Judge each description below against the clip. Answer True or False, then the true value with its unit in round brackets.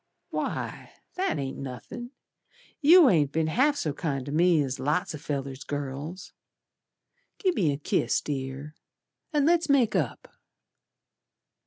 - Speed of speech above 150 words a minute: False (135 wpm)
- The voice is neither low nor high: True (155 Hz)